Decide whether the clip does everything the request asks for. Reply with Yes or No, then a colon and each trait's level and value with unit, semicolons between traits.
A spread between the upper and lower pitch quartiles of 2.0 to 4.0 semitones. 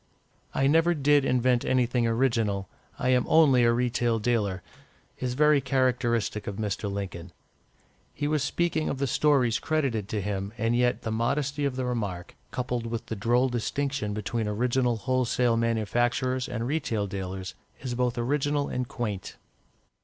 Yes: average, 3.0 semitones